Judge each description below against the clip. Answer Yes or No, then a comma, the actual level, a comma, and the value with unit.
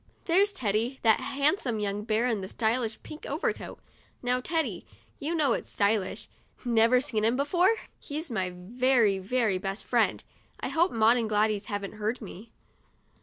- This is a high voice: Yes, high, 230 Hz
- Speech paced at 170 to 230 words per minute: No, average, 160 wpm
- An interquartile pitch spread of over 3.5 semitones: Yes, average, 4.2 semitones